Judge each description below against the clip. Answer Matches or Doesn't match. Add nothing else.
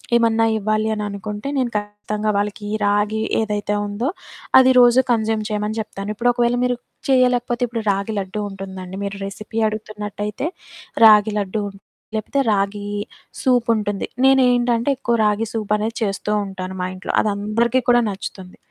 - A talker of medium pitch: Doesn't match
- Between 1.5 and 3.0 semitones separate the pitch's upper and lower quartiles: Matches